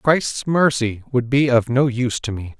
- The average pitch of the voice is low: Yes, low, 125 Hz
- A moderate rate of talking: No, fast, 210 wpm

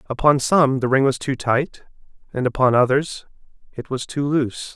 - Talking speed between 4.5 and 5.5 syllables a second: Yes, 5.0 syllables/s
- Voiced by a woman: No, male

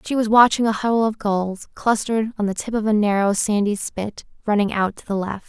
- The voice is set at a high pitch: Yes, high, 210 Hz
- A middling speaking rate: No, fast, 230 wpm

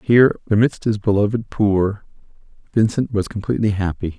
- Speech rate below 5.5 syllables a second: No, 5.6 syllables/s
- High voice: No, low, 105 Hz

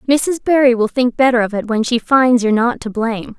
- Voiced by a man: No, female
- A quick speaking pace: Yes, fast, 250 wpm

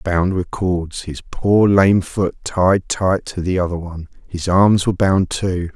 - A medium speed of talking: No, fast, 210 wpm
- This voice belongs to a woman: No, male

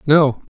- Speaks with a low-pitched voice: No, medium, 145 Hz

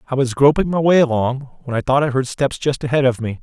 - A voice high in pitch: No, low, 135 Hz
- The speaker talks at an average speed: No, fast, 280 wpm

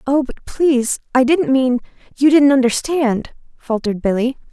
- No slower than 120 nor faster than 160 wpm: Yes, slow, 135 wpm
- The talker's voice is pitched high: Yes, very high, 260 Hz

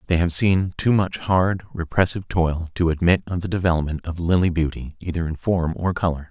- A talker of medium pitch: No, very low, 85 Hz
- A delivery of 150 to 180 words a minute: No, average, 200 wpm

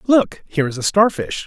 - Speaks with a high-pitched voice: No, medium, 170 Hz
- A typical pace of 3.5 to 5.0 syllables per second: No, 5.4 syllables/s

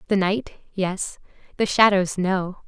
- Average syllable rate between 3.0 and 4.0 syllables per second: Yes, 3.7 syllables/s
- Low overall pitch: No, high, 195 Hz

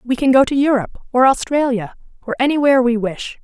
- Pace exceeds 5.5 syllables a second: Yes, 6.4 syllables/s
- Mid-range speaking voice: No, very high, 255 Hz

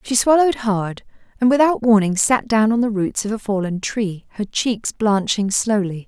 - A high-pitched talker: Yes, high, 215 Hz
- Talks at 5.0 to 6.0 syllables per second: No, 4.7 syllables/s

